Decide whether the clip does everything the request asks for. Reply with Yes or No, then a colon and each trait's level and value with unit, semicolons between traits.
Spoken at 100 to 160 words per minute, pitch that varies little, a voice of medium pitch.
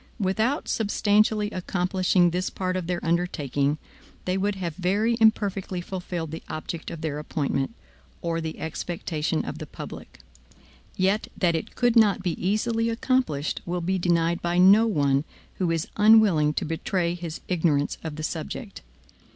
No: average, 150 wpm; average, 3.8 semitones; medium, 180 Hz